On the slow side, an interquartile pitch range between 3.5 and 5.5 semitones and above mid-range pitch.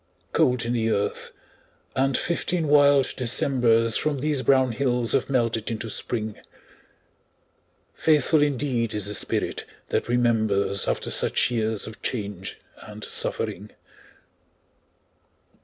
No: slow, 115 wpm; average, 3.8 semitones; low, 120 Hz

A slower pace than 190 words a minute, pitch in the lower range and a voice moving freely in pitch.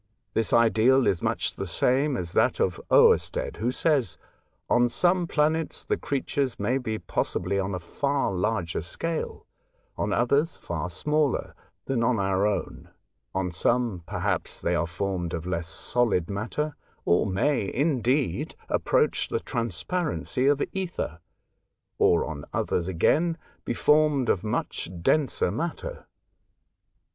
Yes: average, 140 wpm; low, 115 Hz; wide, 7.8 semitones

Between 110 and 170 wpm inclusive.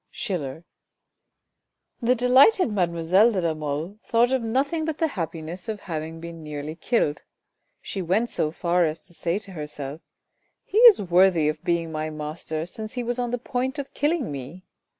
No: average, 180 wpm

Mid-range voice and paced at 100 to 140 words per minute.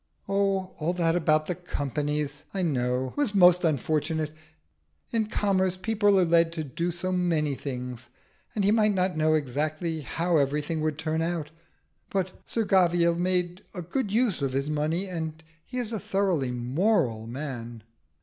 No: medium, 165 Hz; average, 160 wpm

